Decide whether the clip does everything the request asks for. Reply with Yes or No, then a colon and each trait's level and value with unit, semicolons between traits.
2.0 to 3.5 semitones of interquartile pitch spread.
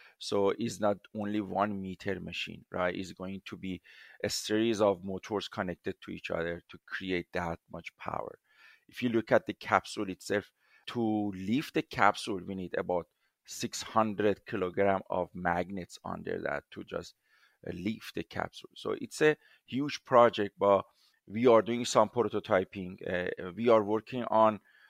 Yes: average, 2.8 semitones